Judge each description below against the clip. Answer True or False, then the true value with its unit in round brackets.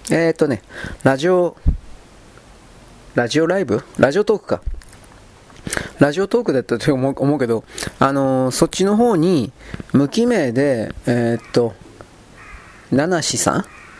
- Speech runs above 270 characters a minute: False (230 characters per minute)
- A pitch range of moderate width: False (6.0 semitones)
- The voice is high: False (135 Hz)